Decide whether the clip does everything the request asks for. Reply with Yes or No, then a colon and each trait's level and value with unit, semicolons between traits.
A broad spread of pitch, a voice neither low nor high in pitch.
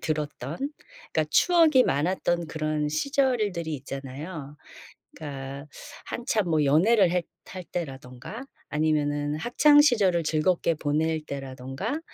Yes: wide, 5.8 semitones; medium, 160 Hz